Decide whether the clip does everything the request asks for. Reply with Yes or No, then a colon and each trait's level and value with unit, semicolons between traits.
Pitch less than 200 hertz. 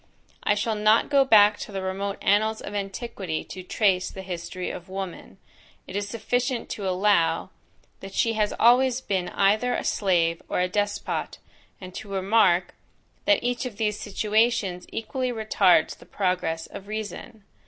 No: high, 205 Hz